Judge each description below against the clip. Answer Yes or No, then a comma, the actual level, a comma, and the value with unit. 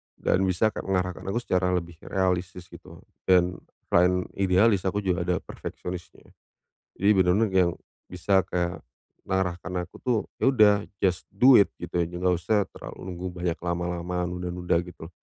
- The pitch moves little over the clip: Yes, narrow, 1.3 semitones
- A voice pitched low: Yes, very low, 90 Hz